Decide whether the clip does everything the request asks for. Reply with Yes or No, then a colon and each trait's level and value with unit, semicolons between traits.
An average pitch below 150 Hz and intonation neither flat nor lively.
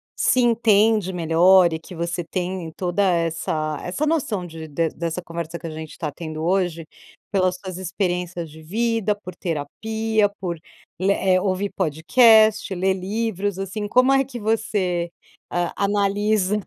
No: medium, 185 Hz; average, 3.7 semitones